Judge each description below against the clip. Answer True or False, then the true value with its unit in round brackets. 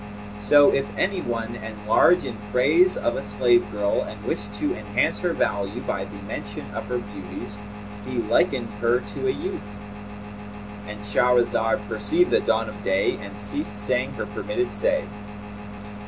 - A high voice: False (105 Hz)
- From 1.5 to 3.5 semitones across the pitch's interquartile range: True (2.9 semitones)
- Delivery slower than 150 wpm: False (155 wpm)